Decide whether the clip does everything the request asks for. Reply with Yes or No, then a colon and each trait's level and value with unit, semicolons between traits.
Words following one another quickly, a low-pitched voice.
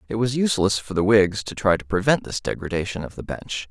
Yes: fast, 245 wpm; low, 105 Hz